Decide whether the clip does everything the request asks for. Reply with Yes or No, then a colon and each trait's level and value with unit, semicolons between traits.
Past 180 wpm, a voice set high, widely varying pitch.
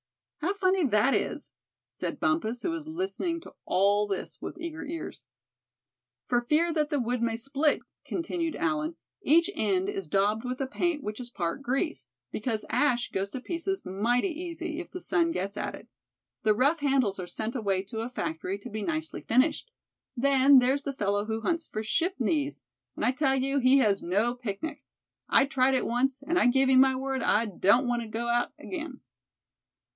Yes: average, 190 wpm; very high, 260 Hz; wide, 6.2 semitones